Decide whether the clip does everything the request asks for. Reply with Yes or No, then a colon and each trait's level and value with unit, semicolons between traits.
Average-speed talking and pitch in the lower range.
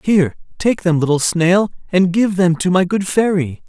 No: average, 195 wpm; medium, 180 Hz